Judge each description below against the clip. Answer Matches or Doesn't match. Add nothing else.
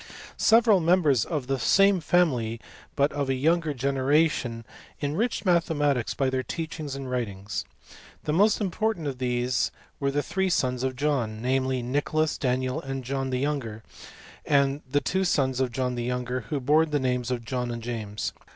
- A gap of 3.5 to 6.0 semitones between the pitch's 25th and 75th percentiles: Matches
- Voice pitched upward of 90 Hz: Matches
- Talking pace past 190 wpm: Doesn't match